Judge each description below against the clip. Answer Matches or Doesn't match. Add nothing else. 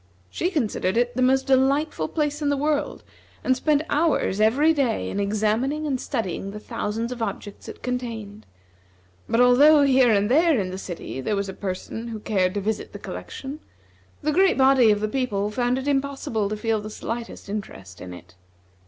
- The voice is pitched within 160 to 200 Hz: Doesn't match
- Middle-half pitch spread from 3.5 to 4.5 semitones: Doesn't match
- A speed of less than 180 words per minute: Doesn't match